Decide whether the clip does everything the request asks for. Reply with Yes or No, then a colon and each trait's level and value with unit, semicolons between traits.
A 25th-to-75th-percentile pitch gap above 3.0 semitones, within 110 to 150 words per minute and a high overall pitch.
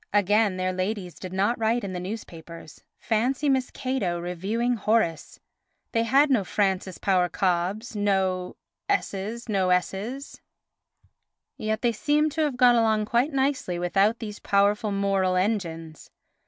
Yes: average, 4.2 semitones; average, 140 wpm; high, 205 Hz